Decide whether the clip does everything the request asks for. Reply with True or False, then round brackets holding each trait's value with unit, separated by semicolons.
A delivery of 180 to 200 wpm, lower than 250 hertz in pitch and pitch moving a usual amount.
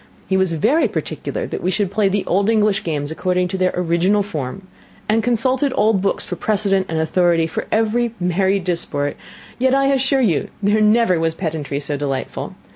True (185 wpm; 190 Hz; 4.4 semitones)